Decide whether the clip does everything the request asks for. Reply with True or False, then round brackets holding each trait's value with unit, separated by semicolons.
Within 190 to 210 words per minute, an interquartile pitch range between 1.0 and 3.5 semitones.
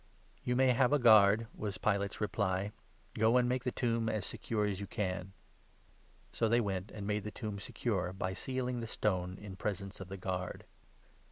True (195 wpm; 3.2 semitones)